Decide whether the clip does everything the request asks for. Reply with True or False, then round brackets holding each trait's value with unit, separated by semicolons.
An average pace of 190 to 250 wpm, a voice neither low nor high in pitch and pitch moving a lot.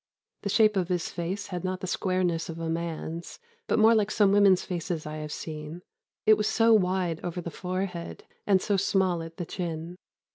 False (195 wpm; 180 Hz; 2.8 semitones)